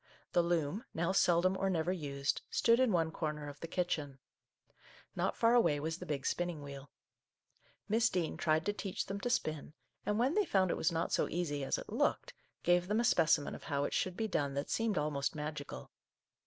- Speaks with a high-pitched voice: No, medium, 170 Hz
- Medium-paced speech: No, fast, 210 wpm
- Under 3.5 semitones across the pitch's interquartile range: No, average, 4.5 semitones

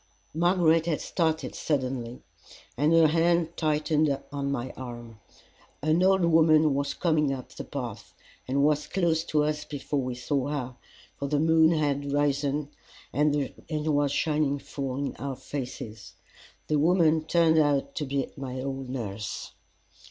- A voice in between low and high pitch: Yes, medium, 145 Hz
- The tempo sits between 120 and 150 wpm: Yes, average, 145 wpm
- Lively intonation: No, narrow, 2.6 semitones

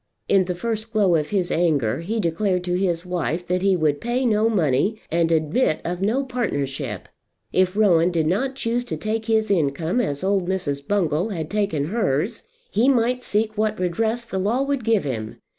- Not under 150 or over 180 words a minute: No, average, 190 wpm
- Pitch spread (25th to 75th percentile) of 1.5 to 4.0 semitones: No, average, 5.3 semitones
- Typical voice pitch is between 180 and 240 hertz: Yes, high, 190 Hz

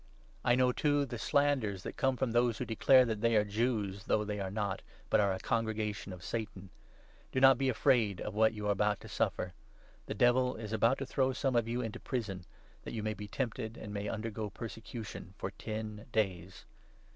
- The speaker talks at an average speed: No, fast, 210 wpm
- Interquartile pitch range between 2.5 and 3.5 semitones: Yes, average, 2.9 semitones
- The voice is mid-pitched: No, low, 110 Hz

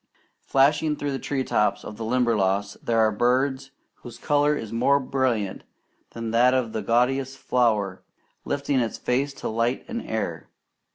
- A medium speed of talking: Yes, average, 160 wpm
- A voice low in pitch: Yes, low, 125 Hz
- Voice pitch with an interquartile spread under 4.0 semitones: Yes, average, 3.5 semitones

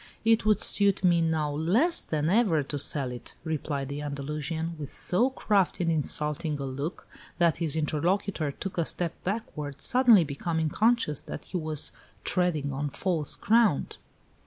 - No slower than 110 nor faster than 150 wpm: No, average, 160 wpm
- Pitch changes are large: No, average, 4.4 semitones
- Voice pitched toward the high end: No, medium, 160 Hz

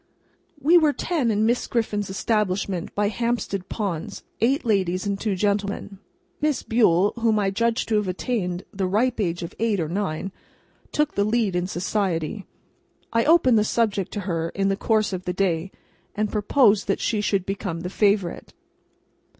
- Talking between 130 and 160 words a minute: No, average, 170 wpm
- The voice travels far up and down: No, average, 3.3 semitones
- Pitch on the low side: No, high, 205 Hz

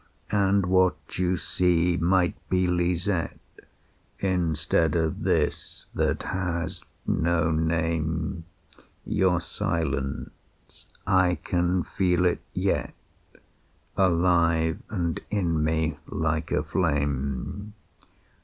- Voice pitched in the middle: No, very low, 85 Hz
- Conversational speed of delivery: No, slow, 90 wpm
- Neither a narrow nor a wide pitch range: No, narrow, 2.2 semitones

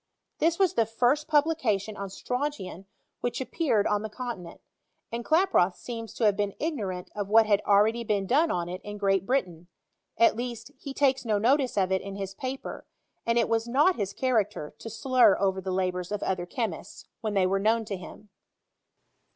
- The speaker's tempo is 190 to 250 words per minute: Yes, average, 195 wpm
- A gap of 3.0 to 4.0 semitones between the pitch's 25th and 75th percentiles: No, average, 4.5 semitones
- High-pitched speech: Yes, high, 215 Hz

